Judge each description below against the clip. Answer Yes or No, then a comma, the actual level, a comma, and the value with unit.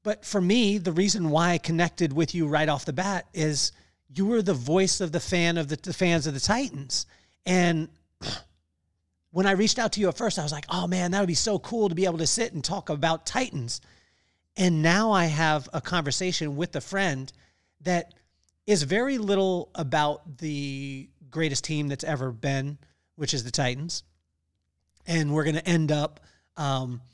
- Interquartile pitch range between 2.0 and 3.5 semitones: No, average, 4.9 semitones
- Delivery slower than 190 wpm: No, average, 195 wpm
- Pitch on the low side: No, medium, 160 Hz